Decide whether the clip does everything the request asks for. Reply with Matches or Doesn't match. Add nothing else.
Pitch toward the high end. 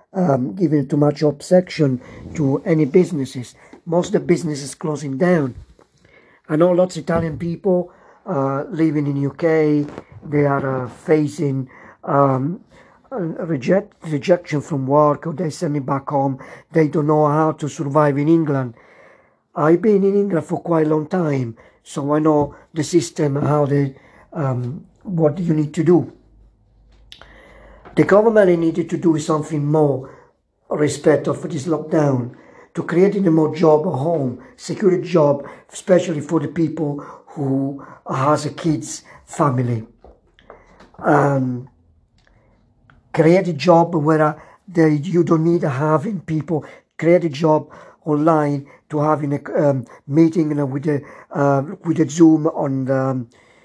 Doesn't match